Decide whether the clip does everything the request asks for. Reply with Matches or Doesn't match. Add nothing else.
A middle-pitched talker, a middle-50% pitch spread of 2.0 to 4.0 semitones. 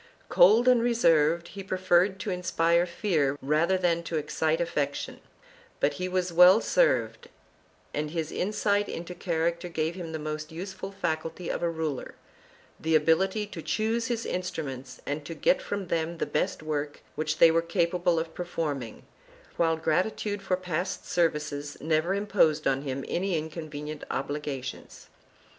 Matches